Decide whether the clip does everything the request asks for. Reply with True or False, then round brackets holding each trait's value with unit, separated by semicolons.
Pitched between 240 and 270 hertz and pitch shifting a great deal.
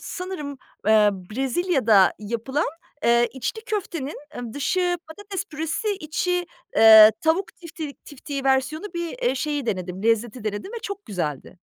False (285 Hz; 7.6 semitones)